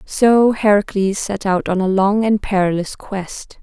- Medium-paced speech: Yes, average, 165 wpm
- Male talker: No, female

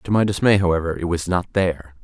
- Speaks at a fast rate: Yes, fast, 235 wpm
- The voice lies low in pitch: Yes, very low, 90 Hz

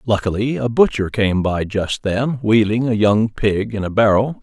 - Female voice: No, male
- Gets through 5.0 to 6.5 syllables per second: No, 4.4 syllables/s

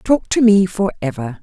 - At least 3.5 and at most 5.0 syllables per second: Yes, 4.6 syllables/s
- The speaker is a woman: Yes, female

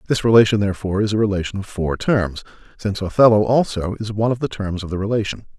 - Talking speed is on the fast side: Yes, fast, 215 wpm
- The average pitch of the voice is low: Yes, low, 105 Hz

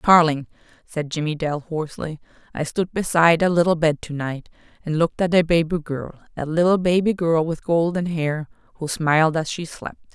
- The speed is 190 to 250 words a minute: No, average, 175 wpm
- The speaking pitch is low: No, medium, 165 Hz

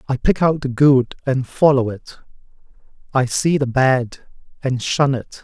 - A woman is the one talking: No, male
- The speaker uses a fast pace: No, average, 165 wpm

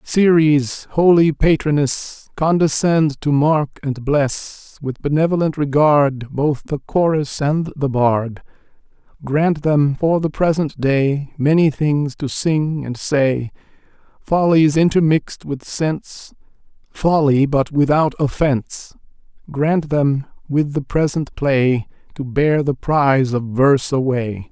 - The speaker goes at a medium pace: No, slow, 120 wpm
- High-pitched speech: No, medium, 145 Hz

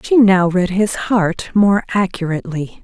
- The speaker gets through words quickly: No, average, 150 wpm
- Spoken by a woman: Yes, female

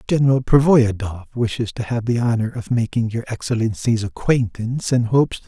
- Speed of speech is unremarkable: Yes, average, 155 wpm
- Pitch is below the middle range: Yes, low, 115 Hz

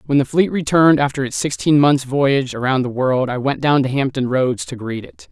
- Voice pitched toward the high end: No, low, 135 Hz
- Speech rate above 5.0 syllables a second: Yes, 5.4 syllables/s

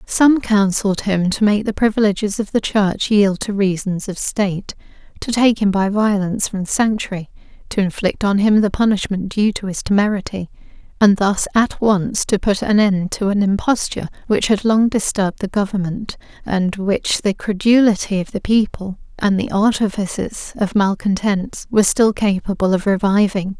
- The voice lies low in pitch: No, high, 200 Hz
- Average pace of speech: Yes, average, 170 wpm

